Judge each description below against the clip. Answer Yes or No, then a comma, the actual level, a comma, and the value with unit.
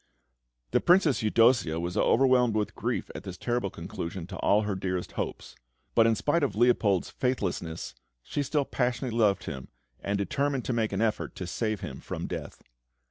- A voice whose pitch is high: No, low, 110 Hz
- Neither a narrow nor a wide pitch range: Yes, average, 4.7 semitones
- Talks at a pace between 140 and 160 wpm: No, average, 175 wpm